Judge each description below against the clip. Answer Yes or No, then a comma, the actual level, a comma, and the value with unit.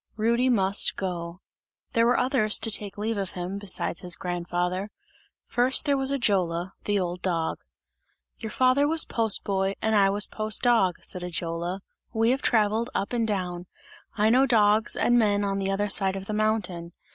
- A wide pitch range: No, average, 3.8 semitones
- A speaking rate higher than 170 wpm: Yes, average, 180 wpm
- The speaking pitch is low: No, high, 205 Hz